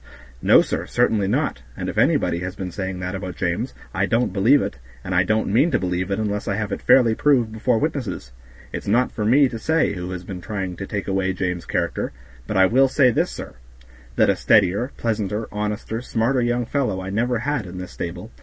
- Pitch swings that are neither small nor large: Yes, average, 4.4 semitones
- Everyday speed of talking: No, fast, 220 wpm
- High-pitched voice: No, low, 105 Hz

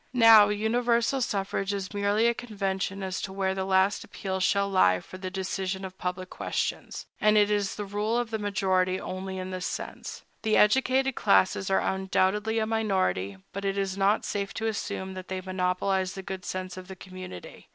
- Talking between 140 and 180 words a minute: No, average, 190 wpm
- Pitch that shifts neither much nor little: No, narrow, 2.0 semitones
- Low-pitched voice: No, high, 195 Hz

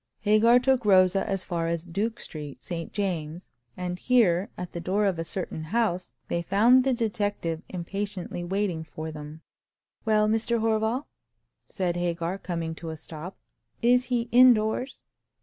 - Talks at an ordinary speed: Yes, average, 150 wpm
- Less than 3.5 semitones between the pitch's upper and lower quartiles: No, average, 4.6 semitones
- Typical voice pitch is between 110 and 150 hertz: No, high, 190 Hz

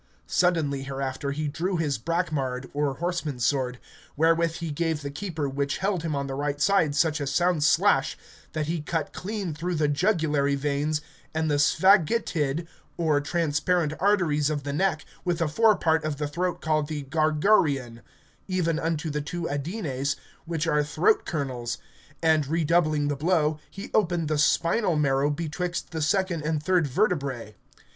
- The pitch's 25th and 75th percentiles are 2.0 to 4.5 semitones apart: Yes, average, 3.0 semitones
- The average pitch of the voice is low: No, medium, 155 Hz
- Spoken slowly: No, average, 165 wpm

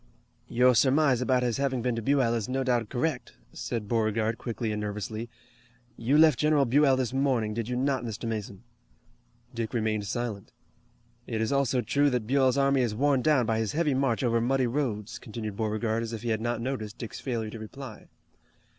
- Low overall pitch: Yes, low, 120 Hz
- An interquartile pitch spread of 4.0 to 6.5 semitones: No, average, 3.2 semitones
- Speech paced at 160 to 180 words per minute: No, average, 190 wpm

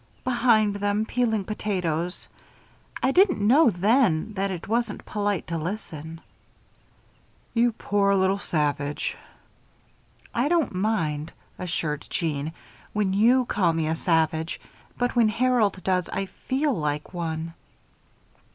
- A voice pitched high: Yes, high, 195 Hz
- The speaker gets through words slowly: Yes, slow, 120 wpm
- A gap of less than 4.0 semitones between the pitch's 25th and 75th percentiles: No, wide, 5.6 semitones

